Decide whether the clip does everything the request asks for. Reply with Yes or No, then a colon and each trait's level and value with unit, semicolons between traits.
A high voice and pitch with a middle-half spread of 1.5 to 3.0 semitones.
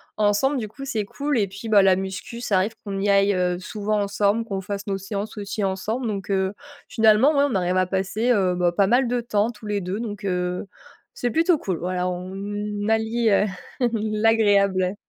Yes: high, 205 Hz; narrow, 2.6 semitones